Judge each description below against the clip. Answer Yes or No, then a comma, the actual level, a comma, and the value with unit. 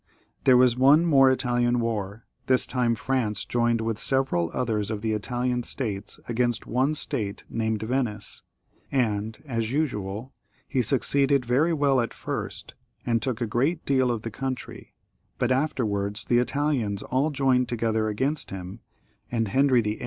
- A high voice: No, low, 120 Hz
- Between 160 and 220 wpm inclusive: No, average, 150 wpm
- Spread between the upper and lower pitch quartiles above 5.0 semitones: No, average, 3.3 semitones